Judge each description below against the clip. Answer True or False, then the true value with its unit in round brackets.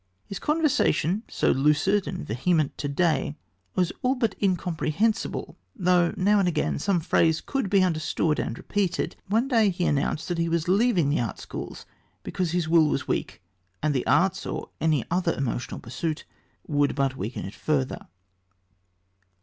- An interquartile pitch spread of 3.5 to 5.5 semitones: True (4.4 semitones)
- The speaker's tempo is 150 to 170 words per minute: True (160 wpm)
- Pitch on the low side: False (170 Hz)